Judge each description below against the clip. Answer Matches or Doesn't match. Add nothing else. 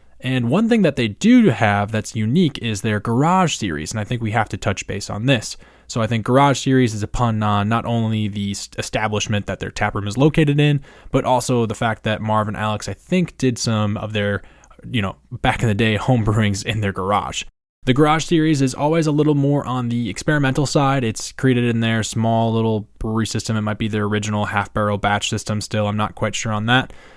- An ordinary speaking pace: Doesn't match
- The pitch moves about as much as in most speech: Matches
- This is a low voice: Matches